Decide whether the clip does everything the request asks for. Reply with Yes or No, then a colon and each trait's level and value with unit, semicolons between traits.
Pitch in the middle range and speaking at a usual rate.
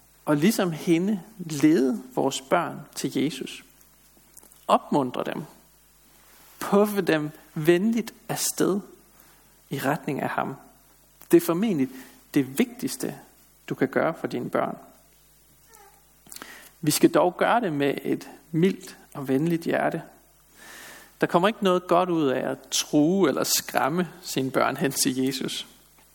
No: medium, 165 Hz; slow, 130 wpm